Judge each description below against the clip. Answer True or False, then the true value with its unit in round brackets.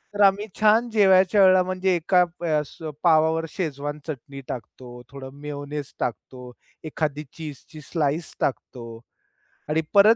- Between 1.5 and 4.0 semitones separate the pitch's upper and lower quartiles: False (4.7 semitones)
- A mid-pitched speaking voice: True (155 Hz)